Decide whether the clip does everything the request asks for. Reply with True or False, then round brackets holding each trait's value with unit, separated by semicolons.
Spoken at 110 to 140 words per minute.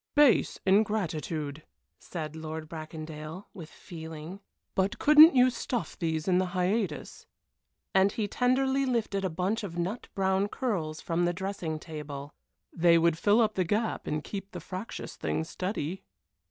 False (150 wpm)